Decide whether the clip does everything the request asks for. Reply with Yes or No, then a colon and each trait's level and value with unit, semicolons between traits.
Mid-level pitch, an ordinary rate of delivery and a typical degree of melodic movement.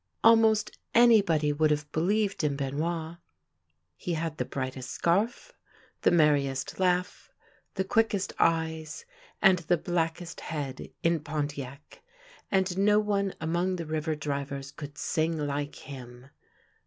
No: medium, 160 Hz; slow, 125 wpm; average, 4.3 semitones